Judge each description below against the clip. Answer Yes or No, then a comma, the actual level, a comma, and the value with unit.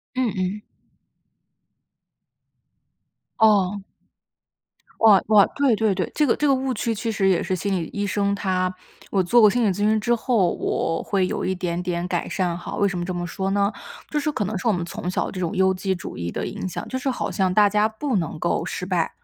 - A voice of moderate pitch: No, high, 195 Hz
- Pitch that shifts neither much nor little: Yes, average, 3.2 semitones